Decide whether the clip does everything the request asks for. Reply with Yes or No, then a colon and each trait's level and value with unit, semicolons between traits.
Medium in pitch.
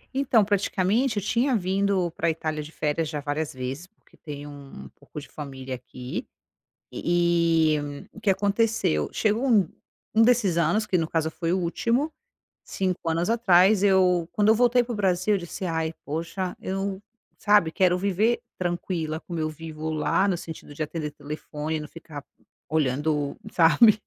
Yes: medium, 175 Hz